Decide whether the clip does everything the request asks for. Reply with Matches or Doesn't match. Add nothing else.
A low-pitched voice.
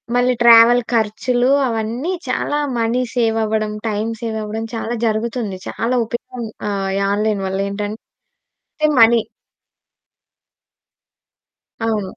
Doesn't match